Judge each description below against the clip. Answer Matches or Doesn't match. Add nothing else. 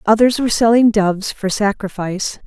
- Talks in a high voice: Matches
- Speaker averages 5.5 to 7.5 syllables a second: Matches